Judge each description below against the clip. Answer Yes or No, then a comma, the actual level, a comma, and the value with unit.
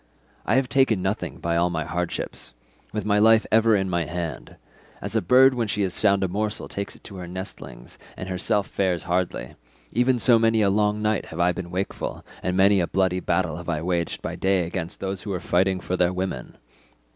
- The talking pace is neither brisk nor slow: No, fast, 210 wpm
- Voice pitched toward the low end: Yes, very low, 95 Hz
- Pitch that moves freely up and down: No, average, 3.1 semitones